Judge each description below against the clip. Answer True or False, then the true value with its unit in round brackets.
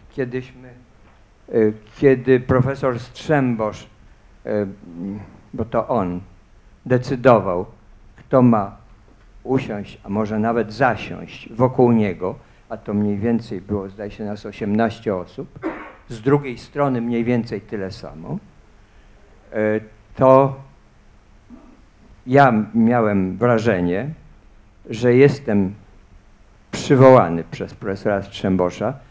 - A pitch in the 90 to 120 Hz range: True (110 Hz)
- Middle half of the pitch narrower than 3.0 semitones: False (3.7 semitones)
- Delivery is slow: True (90 wpm)